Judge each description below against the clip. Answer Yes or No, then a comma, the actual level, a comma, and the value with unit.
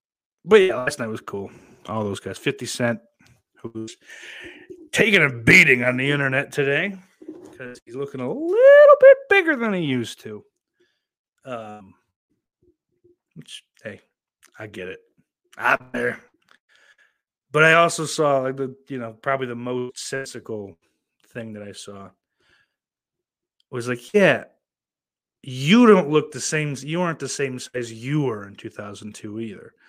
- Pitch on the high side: No, low, 135 Hz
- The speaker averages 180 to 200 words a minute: No, average, 145 wpm